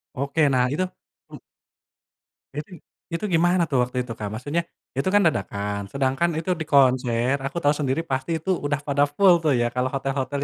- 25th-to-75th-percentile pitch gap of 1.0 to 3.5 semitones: No, average, 4.3 semitones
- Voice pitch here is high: No, medium, 140 Hz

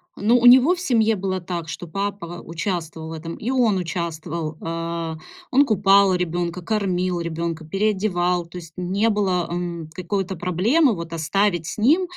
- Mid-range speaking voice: Yes, medium, 180 Hz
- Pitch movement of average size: Yes, average, 3.6 semitones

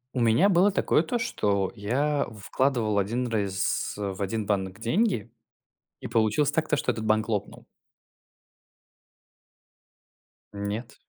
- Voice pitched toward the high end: No, low, 115 Hz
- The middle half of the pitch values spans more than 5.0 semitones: Yes, wide, 5.6 semitones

